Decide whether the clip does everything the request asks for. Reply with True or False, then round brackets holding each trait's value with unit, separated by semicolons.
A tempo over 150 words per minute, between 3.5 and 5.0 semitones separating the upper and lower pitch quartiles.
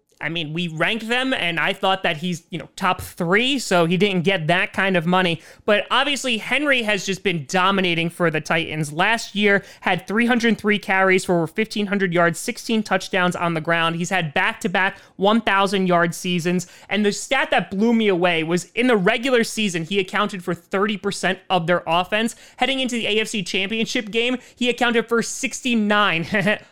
True (175 wpm; 3.9 semitones)